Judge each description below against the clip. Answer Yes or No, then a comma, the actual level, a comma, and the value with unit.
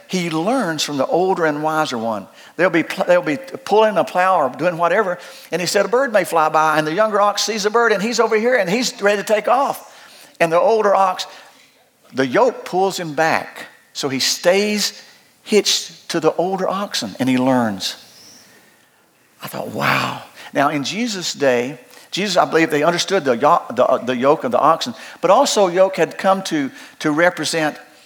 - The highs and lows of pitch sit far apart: No, average, 4.7 semitones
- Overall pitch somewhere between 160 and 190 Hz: Yes, medium, 185 Hz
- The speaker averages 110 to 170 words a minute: No, average, 190 wpm